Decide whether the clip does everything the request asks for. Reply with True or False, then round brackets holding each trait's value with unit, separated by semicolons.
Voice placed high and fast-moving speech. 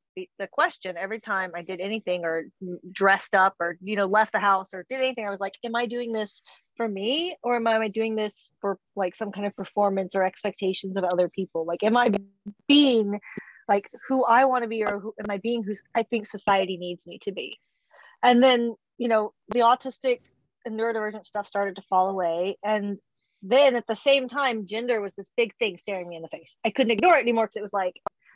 True (205 Hz; 225 wpm)